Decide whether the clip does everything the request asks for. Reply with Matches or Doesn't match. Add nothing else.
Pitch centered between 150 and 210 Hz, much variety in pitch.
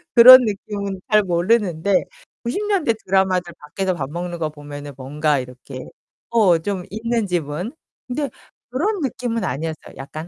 Matches